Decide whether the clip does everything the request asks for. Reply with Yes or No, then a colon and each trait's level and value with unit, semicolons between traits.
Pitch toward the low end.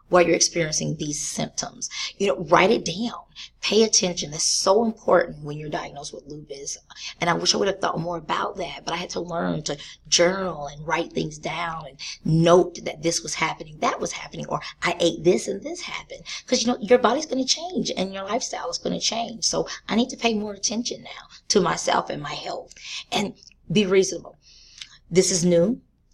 No: medium, 180 Hz